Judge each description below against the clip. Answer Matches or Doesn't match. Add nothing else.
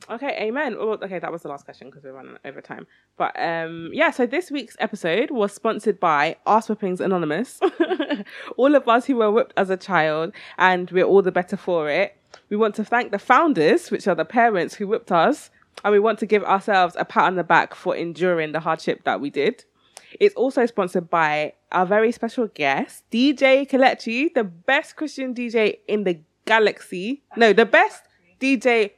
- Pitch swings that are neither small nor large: Doesn't match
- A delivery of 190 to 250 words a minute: Matches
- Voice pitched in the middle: Doesn't match